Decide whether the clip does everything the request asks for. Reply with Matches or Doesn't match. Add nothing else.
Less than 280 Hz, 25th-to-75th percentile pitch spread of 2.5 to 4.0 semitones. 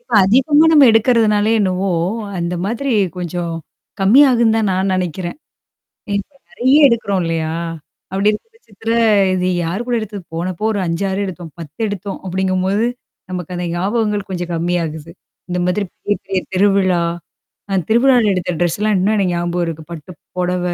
Matches